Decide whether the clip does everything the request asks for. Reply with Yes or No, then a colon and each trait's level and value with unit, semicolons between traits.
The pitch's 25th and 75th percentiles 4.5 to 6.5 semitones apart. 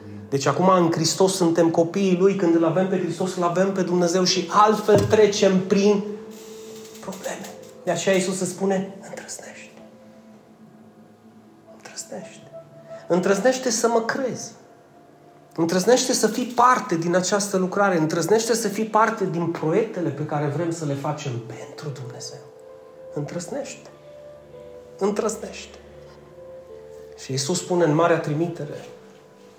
Yes: average, 5.0 semitones